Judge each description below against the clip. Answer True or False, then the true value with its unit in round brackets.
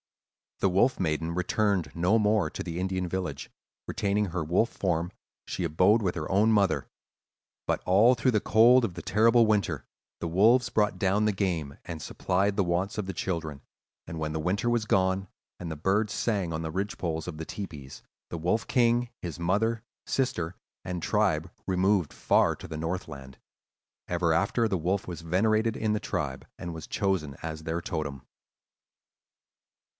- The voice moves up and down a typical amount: True (4.2 semitones)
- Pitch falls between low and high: False (95 Hz)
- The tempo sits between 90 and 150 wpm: False (175 wpm)